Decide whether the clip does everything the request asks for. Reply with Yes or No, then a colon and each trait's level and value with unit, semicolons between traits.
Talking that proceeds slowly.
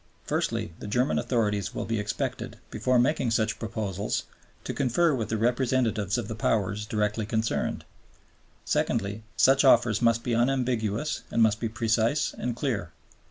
No: average, 150 wpm